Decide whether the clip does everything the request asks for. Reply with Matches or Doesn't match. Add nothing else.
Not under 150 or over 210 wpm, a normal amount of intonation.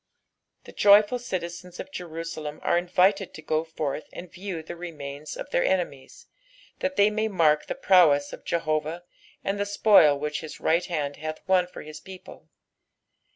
Matches